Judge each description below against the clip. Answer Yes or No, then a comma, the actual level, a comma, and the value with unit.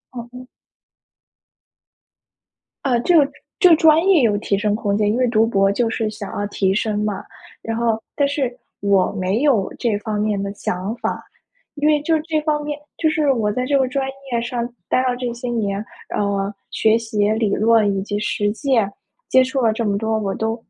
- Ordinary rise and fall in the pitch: Yes, average, 4.0 semitones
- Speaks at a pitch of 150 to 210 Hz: No, high, 225 Hz